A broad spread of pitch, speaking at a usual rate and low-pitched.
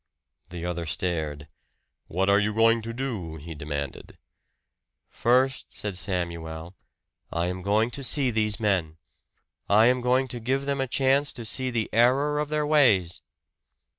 Yes: wide, 6.8 semitones; average, 155 wpm; low, 110 Hz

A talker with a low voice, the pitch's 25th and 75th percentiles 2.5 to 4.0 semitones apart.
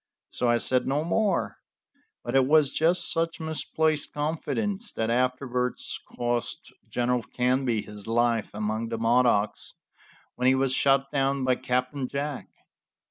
Yes: low, 130 Hz; average, 3.6 semitones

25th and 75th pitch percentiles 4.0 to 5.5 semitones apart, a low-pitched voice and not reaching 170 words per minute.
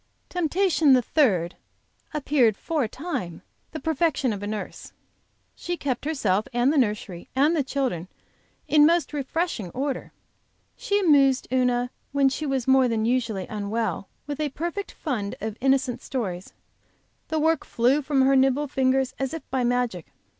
No: average, 4.5 semitones; very high, 265 Hz; average, 155 wpm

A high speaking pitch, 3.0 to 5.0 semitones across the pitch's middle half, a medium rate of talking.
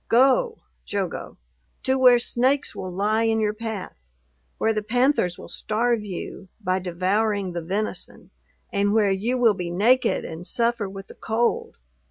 Yes: high, 215 Hz; average, 3.9 semitones; average, 155 wpm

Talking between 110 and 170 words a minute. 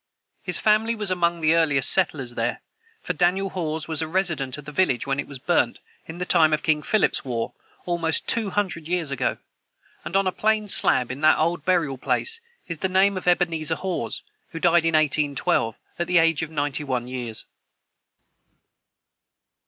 No: average, 185 wpm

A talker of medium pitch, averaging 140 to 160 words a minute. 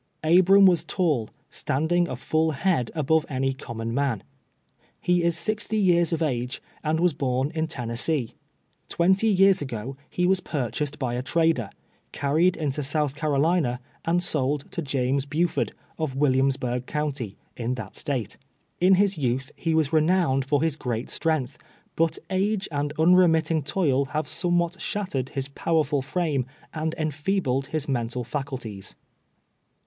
Yes: medium, 150 Hz; average, 145 wpm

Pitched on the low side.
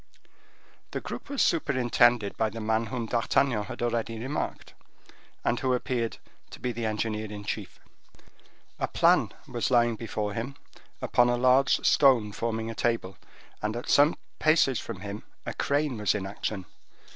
Yes: low, 115 Hz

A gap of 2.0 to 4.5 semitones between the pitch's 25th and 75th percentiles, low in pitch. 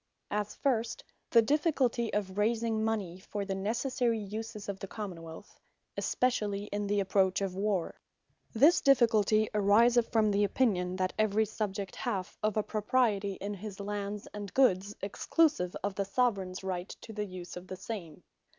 No: narrow, 2.6 semitones; high, 205 Hz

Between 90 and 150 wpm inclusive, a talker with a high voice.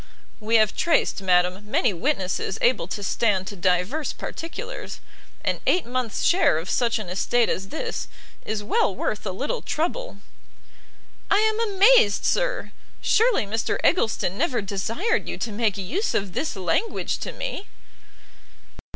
Yes: average, 145 wpm; high, 225 Hz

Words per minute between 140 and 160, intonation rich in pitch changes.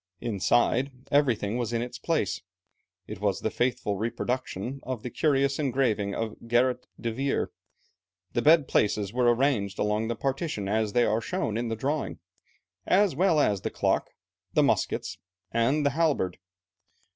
No: average, 155 wpm; average, 4.1 semitones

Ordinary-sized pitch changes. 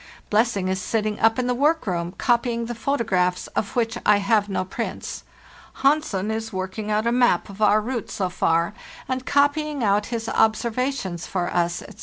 Yes: average, 4.1 semitones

